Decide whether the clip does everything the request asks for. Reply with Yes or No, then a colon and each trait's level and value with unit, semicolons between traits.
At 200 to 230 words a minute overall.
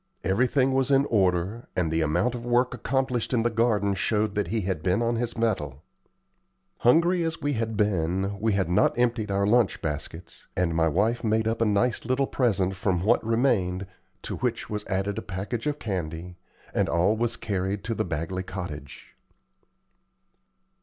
No: average, 175 wpm